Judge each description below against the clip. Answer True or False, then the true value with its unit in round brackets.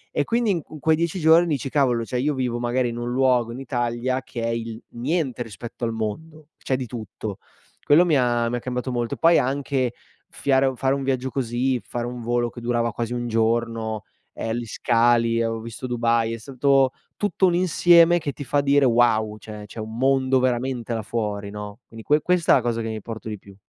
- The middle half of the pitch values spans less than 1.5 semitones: False (2.9 semitones)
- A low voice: True (120 Hz)